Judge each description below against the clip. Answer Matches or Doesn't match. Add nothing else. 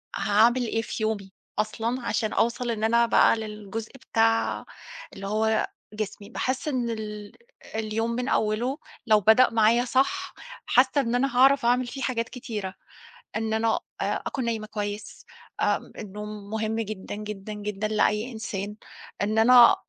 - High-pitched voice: Matches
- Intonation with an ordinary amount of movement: Doesn't match